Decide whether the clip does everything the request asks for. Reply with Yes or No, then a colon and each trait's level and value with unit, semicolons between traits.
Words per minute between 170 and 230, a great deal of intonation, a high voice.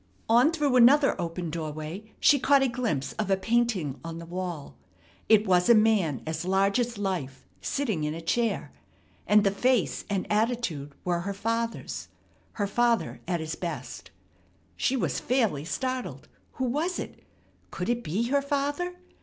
No: average, 160 wpm; wide, 6.2 semitones; high, 210 Hz